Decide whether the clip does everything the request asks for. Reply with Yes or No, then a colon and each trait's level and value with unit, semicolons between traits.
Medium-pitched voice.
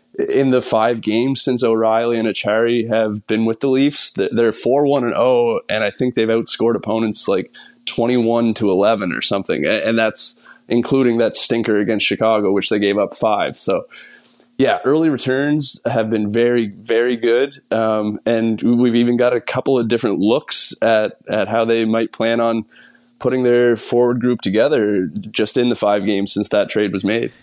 No: low, 115 Hz